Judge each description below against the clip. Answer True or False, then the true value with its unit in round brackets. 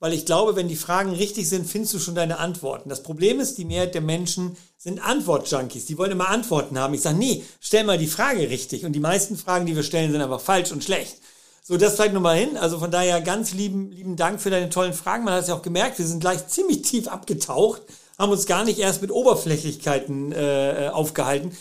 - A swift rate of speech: True (235 wpm)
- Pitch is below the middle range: False (180 Hz)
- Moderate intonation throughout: True (3.6 semitones)